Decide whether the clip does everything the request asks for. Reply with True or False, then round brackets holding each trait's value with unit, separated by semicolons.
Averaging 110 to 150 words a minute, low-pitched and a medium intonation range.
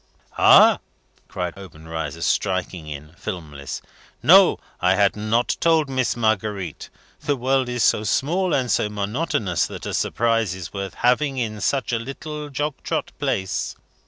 False (145 wpm; 110 Hz; 6.2 semitones)